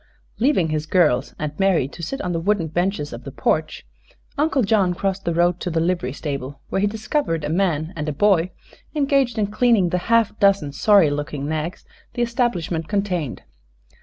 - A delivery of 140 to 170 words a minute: No, average, 185 wpm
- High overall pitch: No, medium, 180 Hz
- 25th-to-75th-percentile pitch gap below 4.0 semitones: No, average, 5.0 semitones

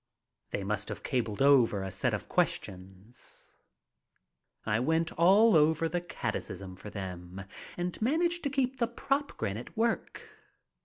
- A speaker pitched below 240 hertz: Yes, medium, 140 Hz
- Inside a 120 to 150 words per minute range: Yes, average, 145 wpm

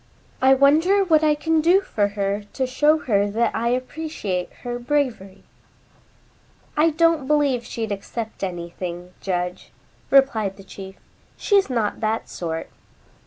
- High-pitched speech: Yes, high, 240 Hz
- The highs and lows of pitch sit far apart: Yes, wide, 7.1 semitones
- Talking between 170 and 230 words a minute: No, slow, 135 wpm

